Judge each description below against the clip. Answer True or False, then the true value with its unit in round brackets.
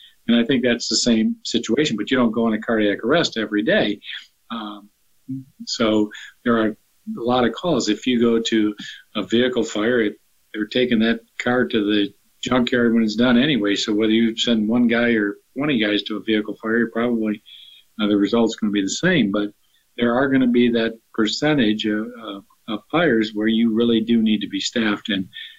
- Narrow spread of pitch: True (2.0 semitones)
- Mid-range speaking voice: False (115 Hz)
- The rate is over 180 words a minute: True (205 wpm)